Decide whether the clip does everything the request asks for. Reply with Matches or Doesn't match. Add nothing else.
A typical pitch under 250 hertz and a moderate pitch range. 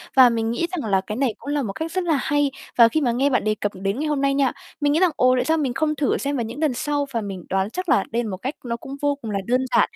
Doesn't match